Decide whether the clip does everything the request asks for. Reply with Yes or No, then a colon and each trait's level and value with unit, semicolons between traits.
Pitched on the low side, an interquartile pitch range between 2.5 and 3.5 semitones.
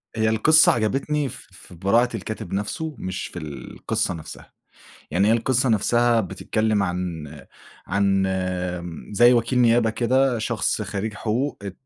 No: low, 110 Hz; average, 3.9 semitones